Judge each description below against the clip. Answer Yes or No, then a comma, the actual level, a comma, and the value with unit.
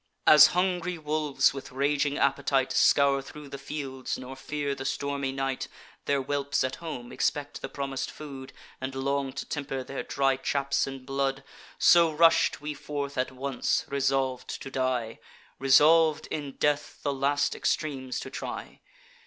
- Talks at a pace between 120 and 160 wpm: Yes, average, 155 wpm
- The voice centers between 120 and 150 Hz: Yes, medium, 140 Hz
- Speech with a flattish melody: Yes, narrow, 1.6 semitones